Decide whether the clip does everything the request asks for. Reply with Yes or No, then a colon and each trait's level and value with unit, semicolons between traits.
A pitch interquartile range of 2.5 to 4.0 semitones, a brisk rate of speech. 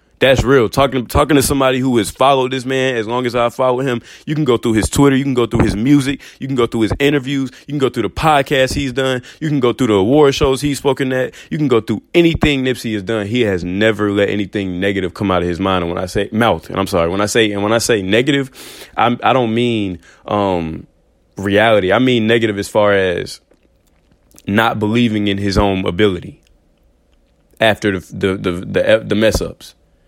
No: average, 4.7 semitones; fast, 225 wpm